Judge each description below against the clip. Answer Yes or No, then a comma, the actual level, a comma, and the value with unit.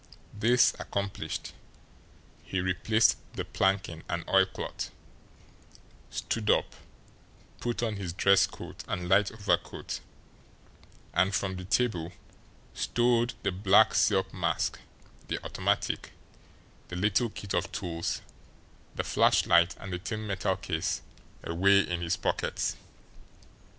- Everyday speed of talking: No, slow, 115 wpm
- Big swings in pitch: No, average, 3.1 semitones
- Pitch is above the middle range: No, very low, 95 Hz